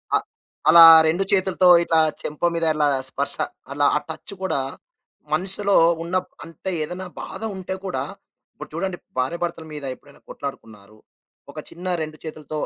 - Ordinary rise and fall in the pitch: Yes, average, 3.8 semitones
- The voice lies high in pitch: No, medium, 165 Hz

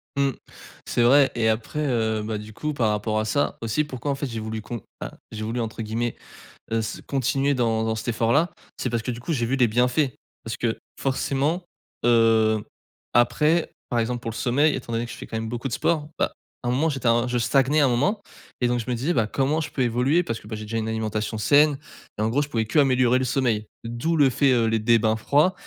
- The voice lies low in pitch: Yes, low, 120 Hz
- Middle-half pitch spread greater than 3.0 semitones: Yes, average, 3.6 semitones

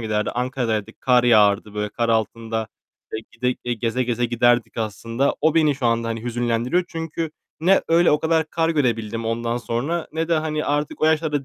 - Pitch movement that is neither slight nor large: Yes, average, 5.0 semitones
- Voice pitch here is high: No, low, 120 Hz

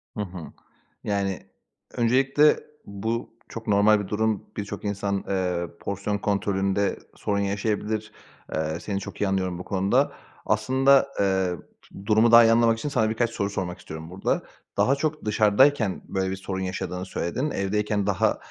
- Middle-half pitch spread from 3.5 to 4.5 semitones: No, narrow, 2.6 semitones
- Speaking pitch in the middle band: No, low, 100 Hz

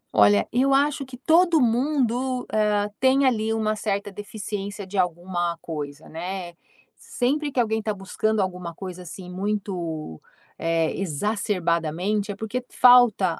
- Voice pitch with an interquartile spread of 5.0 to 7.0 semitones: Yes, wide, 5.4 semitones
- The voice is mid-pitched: No, high, 205 Hz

